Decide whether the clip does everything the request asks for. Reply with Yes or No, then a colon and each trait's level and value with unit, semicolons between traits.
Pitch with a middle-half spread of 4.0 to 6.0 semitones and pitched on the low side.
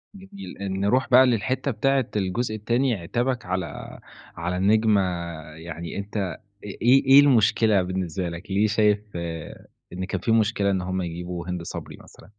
Yes: average, 5.0 semitones; low, 100 Hz